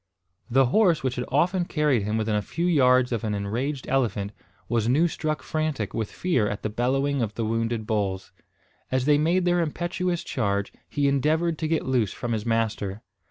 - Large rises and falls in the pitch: Yes, wide, 5.9 semitones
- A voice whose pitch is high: No, low, 130 Hz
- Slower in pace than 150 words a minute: No, average, 190 wpm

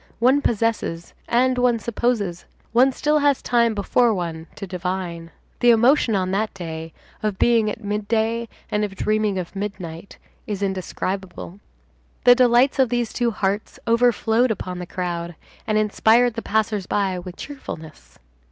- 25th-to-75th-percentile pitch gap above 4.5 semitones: No, average, 4.2 semitones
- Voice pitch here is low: No, high, 215 Hz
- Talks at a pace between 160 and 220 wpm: No, average, 150 wpm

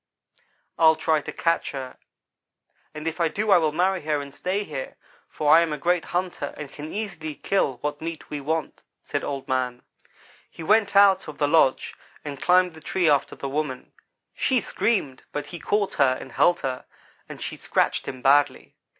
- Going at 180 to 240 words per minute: Yes, average, 190 wpm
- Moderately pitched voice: Yes, medium, 155 Hz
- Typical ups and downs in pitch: Yes, average, 4.0 semitones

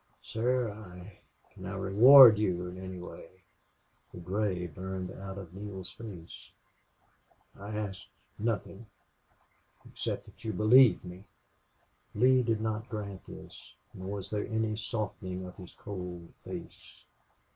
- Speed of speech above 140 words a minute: No, slow, 135 wpm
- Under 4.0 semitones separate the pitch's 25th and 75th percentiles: Yes, average, 2.9 semitones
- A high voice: No, low, 100 Hz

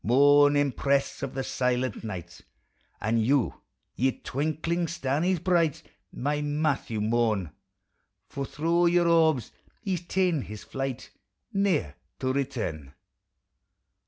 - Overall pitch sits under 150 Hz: Yes, medium, 140 Hz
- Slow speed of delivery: Yes, slow, 115 wpm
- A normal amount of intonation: Yes, average, 5.0 semitones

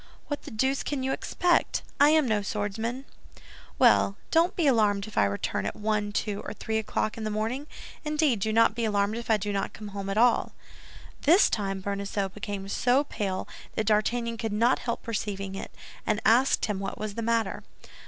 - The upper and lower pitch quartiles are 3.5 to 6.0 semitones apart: No, average, 3.1 semitones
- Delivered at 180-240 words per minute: Yes, average, 195 wpm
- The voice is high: Yes, high, 215 Hz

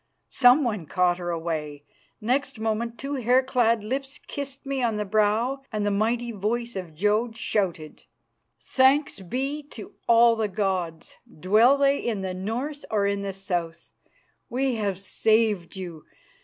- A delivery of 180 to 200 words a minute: No, average, 150 wpm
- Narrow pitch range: No, average, 4.7 semitones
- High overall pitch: Yes, high, 220 Hz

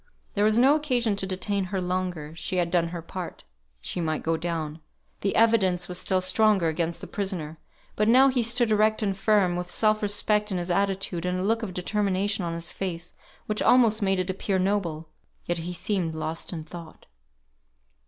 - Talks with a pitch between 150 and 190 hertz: Yes, medium, 185 Hz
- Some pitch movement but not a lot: Yes, average, 3.5 semitones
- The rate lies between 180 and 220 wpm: Yes, average, 190 wpm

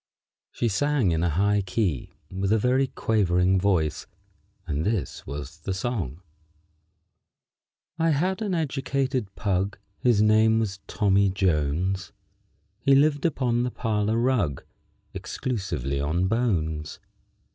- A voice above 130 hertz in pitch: No, low, 100 Hz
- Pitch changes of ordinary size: No, wide, 5.8 semitones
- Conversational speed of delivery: No, slow, 125 wpm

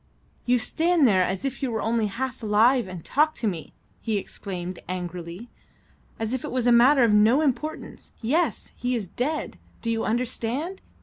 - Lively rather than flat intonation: No, average, 4.1 semitones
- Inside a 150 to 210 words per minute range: Yes, average, 180 wpm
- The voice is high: Yes, high, 235 Hz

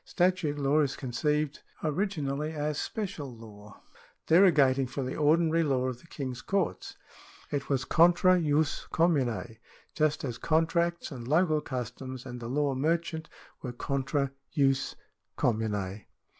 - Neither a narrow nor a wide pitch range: Yes, average, 3.9 semitones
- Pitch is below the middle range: No, medium, 145 Hz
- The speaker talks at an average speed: No, slow, 130 wpm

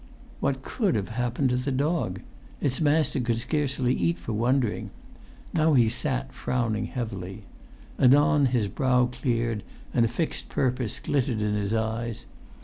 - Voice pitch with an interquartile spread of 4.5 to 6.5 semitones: No, average, 3.4 semitones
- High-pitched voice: No, low, 125 Hz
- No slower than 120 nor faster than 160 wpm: Yes, average, 145 wpm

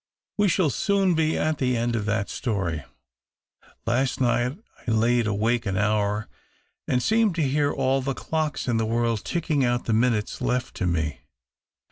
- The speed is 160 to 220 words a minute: Yes, average, 170 wpm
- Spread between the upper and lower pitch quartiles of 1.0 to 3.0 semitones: No, average, 4.8 semitones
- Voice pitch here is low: Yes, low, 120 Hz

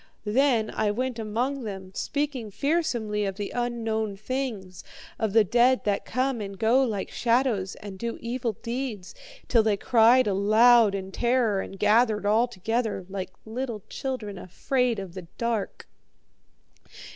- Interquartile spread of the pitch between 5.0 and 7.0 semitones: No, average, 3.4 semitones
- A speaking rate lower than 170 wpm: Yes, average, 145 wpm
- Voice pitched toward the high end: Yes, high, 225 Hz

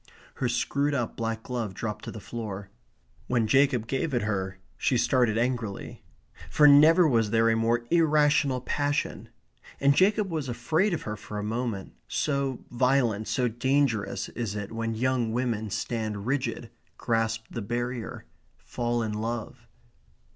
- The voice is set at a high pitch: No, low, 120 Hz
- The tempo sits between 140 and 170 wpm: Yes, average, 150 wpm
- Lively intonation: No, average, 3.5 semitones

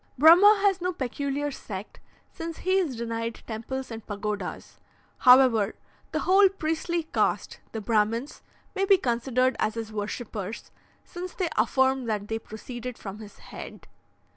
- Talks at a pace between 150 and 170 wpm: No, average, 140 wpm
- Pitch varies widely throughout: Yes, wide, 6.8 semitones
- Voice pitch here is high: Yes, very high, 250 Hz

